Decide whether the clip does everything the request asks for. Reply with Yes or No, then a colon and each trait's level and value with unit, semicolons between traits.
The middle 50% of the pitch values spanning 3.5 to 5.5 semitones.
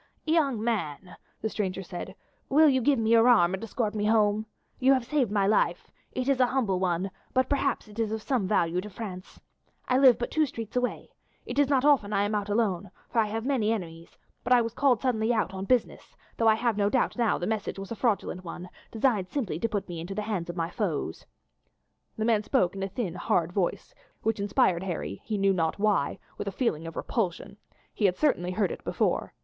Yes: average, 4.2 semitones